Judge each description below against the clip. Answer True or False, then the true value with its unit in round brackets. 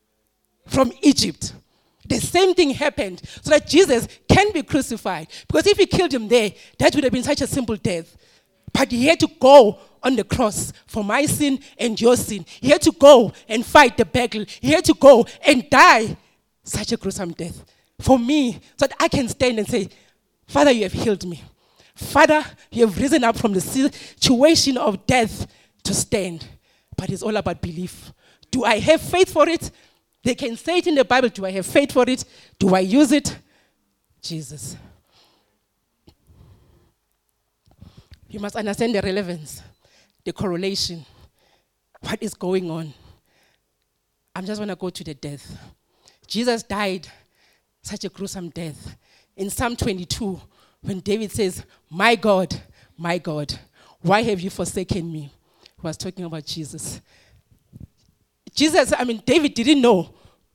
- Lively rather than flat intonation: True (7.0 semitones)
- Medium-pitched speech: False (215 Hz)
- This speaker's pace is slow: False (165 wpm)